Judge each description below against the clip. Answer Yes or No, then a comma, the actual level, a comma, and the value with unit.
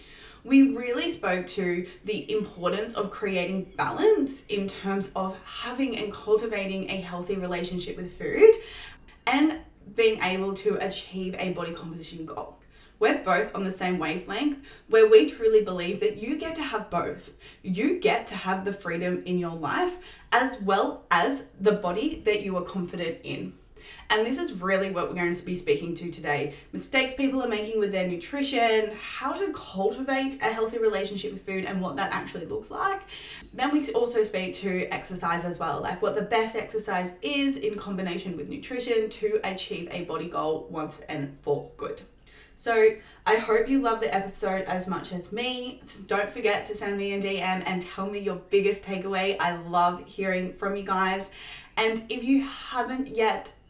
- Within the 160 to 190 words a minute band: Yes, average, 180 wpm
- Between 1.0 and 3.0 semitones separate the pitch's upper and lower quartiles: No, average, 4.3 semitones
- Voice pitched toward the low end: No, high, 200 Hz